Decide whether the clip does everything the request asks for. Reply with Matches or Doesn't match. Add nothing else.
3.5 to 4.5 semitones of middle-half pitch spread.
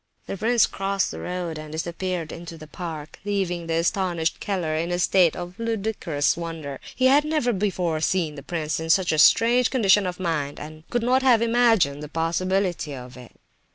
Matches